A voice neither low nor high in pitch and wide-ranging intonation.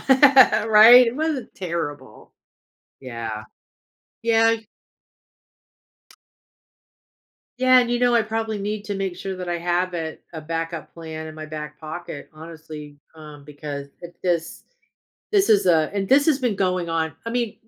Yes: medium, 180 Hz; wide, 6.2 semitones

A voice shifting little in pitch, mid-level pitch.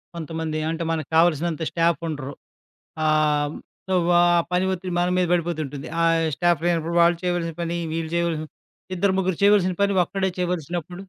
Yes: narrow, 2.1 semitones; medium, 170 Hz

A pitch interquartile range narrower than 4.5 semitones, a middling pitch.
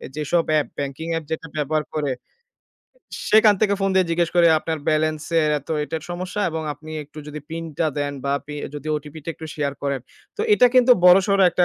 Yes: average, 2.9 semitones; medium, 155 Hz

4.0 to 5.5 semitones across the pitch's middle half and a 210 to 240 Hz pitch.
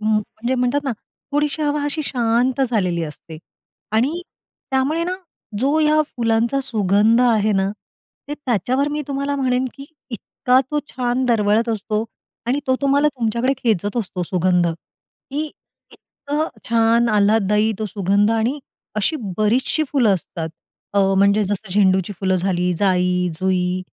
Yes: average, 4.9 semitones; high, 225 Hz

